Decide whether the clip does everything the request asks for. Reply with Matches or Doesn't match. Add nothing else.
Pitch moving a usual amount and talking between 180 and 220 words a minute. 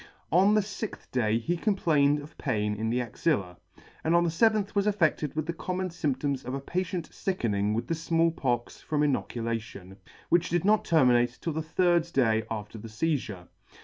Doesn't match